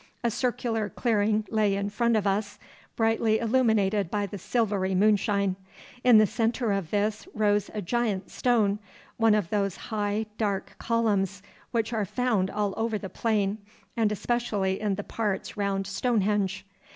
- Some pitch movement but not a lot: No, narrow, 2.2 semitones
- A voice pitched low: No, high, 210 Hz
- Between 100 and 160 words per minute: Yes, average, 150 wpm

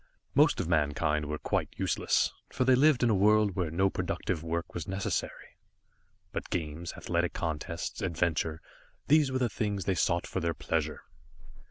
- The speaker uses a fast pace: No, average, 165 wpm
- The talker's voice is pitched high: No, very low, 85 Hz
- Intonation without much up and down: No, average, 4.6 semitones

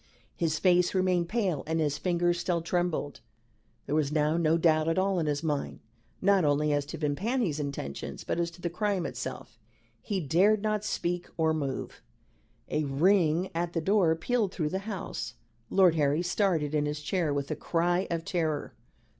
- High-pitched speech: No, medium, 165 Hz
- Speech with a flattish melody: No, average, 3.4 semitones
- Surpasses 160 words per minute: Yes, average, 180 wpm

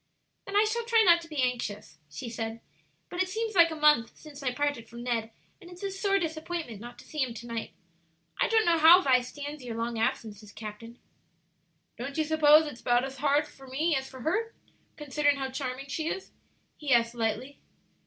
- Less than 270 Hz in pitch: No, very high, 280 Hz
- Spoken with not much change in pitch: No, wide, 5.5 semitones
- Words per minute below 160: No, fast, 205 wpm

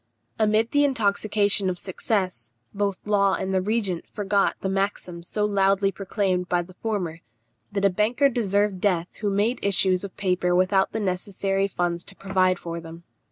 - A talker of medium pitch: No, high, 195 Hz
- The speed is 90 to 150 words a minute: No, average, 165 wpm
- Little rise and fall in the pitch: Yes, narrow, 2.0 semitones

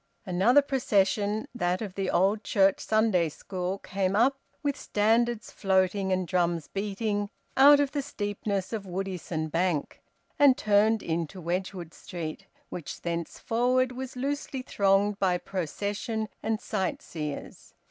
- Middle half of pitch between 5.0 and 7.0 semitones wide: No, average, 3.6 semitones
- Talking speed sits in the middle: No, slow, 125 wpm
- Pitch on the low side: No, high, 200 Hz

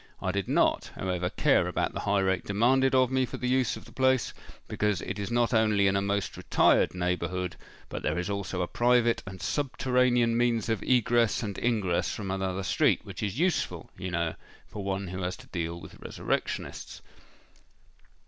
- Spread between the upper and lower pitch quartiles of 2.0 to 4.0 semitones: No, average, 4.5 semitones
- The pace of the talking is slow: No, average, 185 wpm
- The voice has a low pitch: Yes, low, 100 Hz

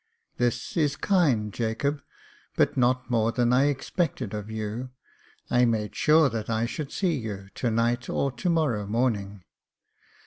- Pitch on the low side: Yes, low, 120 Hz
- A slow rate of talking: No, average, 160 wpm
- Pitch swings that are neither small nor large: Yes, average, 4.1 semitones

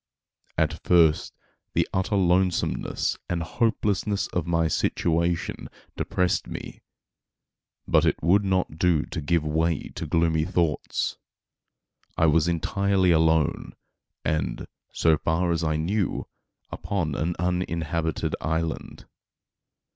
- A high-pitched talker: No, very low, 85 Hz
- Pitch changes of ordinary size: No, narrow, 2.1 semitones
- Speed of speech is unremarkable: No, slow, 110 wpm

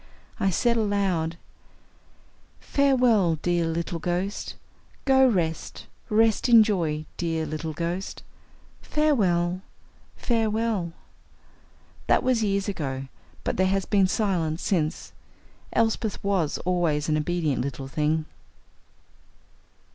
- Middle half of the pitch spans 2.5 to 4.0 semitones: No, average, 4.9 semitones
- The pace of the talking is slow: Yes, slow, 100 wpm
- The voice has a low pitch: No, medium, 180 Hz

